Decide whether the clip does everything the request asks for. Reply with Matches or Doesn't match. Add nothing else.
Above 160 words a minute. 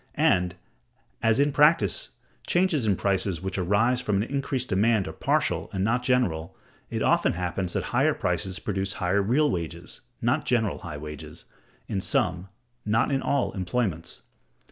Doesn't match